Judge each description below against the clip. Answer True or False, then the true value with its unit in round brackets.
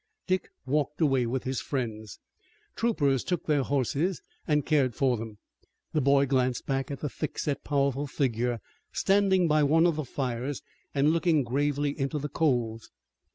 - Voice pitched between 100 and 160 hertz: True (140 Hz)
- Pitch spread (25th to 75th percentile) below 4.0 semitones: True (2.9 semitones)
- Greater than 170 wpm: False (155 wpm)